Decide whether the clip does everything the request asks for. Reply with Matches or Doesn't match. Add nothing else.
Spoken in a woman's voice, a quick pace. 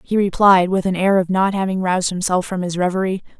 Matches